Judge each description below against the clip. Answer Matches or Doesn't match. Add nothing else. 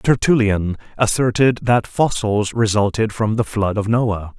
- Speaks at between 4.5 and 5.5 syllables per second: Doesn't match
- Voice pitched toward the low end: Matches